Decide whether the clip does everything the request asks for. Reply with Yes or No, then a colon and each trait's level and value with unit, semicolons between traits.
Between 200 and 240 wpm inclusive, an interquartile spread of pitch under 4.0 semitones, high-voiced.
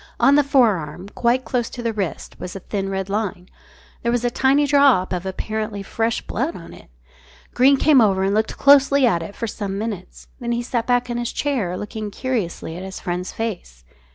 No: fast, 205 wpm; average, 4.5 semitones; high, 220 Hz